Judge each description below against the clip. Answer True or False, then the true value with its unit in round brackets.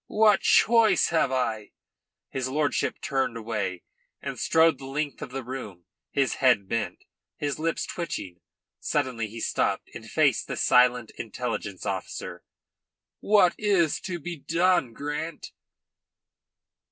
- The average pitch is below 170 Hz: True (135 Hz)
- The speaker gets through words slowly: True (130 wpm)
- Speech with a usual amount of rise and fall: False (6.1 semitones)